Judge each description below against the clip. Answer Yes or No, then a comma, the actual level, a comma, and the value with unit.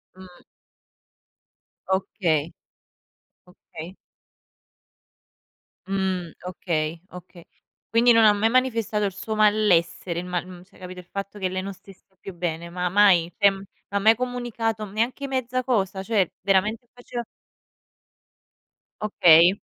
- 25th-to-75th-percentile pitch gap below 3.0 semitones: No, average, 3.4 semitones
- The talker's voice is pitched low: No, high, 195 Hz